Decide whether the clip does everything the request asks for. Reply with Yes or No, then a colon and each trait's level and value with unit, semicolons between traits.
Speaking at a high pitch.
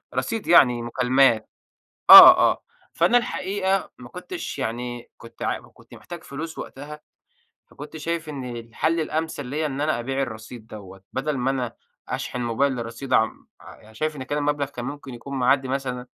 No: low, 135 Hz